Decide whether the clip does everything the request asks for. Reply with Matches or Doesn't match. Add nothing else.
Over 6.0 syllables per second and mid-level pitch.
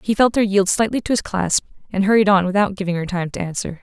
Doesn't match